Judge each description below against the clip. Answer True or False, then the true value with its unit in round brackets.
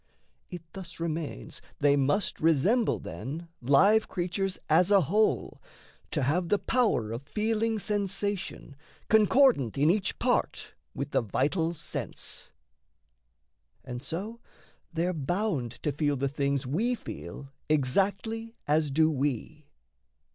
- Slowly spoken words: True (120 wpm)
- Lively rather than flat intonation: True (6.4 semitones)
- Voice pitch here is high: False (165 Hz)